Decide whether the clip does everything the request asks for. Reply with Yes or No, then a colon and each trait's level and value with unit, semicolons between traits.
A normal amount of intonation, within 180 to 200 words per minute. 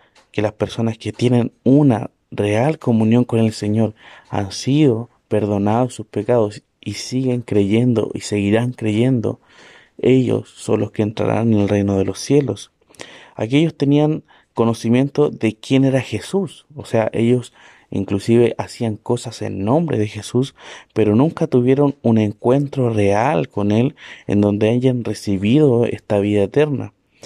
No: average, 3.5 semitones; average, 145 wpm